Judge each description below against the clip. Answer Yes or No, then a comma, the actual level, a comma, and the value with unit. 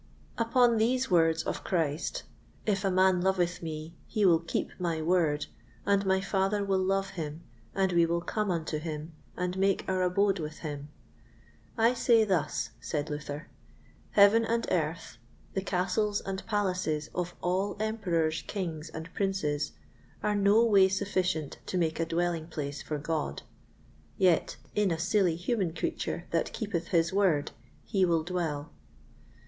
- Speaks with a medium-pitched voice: Yes, medium, 180 Hz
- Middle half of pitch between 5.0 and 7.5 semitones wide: No, average, 3.6 semitones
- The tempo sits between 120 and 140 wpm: No, average, 155 wpm